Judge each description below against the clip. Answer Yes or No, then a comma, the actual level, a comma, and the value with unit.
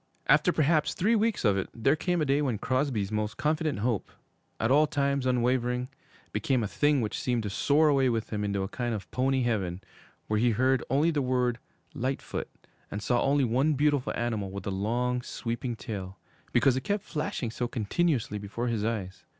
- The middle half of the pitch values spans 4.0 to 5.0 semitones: Yes, average, 4.4 semitones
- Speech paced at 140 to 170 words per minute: No, average, 190 wpm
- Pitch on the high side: No, low, 125 Hz